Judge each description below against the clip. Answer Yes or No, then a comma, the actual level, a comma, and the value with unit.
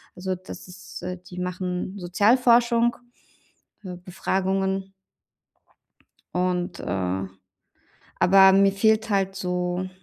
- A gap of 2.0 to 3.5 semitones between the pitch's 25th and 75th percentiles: No, narrow, 1.5 semitones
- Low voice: No, medium, 185 Hz